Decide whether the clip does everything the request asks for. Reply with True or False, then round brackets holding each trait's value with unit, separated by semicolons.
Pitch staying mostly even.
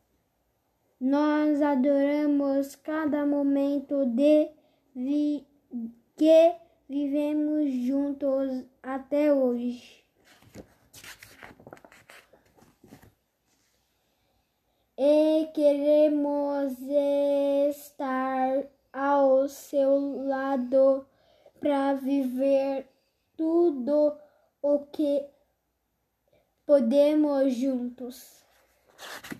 True (1.6 semitones)